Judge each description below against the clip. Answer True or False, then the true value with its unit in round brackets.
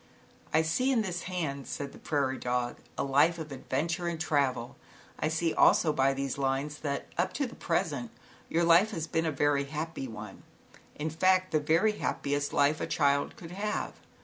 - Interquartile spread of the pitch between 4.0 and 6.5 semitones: False (3.5 semitones)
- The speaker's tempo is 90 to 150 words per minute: False (185 wpm)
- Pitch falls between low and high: True (155 Hz)